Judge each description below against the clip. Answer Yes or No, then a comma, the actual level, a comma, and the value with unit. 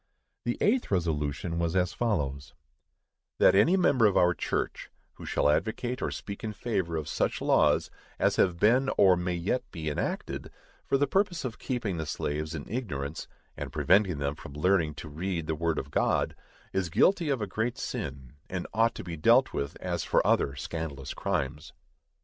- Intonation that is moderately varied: No, wide, 6.7 semitones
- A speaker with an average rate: Yes, average, 180 wpm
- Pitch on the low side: Yes, very low, 90 Hz